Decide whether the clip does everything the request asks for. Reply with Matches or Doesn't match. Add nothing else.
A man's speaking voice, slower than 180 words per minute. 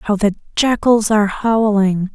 Doesn't match